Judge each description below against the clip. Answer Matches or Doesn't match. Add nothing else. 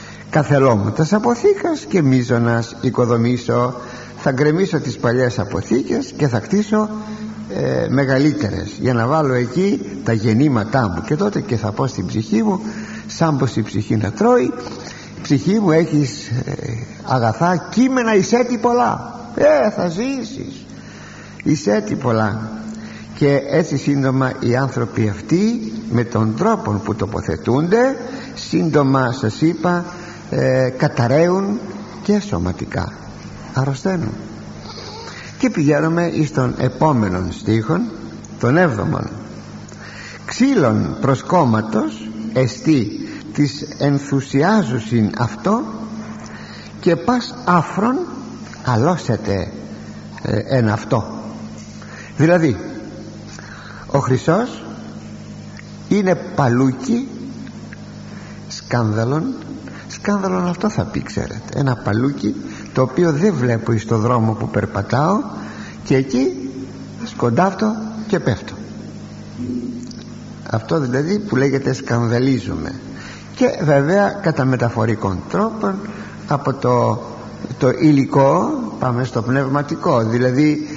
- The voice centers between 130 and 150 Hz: Matches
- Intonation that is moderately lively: Doesn't match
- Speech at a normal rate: Doesn't match